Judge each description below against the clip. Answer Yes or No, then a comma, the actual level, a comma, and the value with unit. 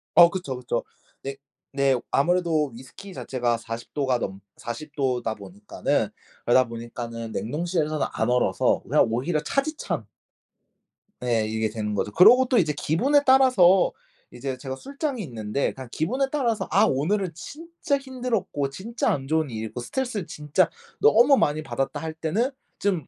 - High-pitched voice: No, medium, 150 Hz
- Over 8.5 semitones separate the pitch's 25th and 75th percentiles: Yes, wide, 9.0 semitones